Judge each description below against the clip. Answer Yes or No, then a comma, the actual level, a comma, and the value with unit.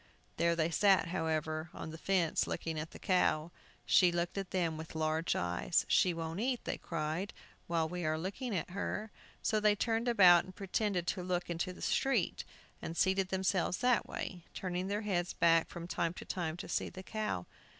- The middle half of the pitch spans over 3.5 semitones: No, average, 2.9 semitones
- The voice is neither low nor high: Yes, medium, 175 Hz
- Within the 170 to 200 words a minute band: Yes, average, 190 wpm